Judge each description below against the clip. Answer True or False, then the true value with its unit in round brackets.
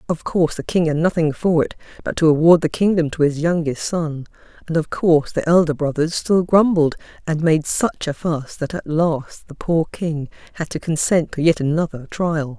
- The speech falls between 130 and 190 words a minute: False (205 wpm)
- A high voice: False (160 Hz)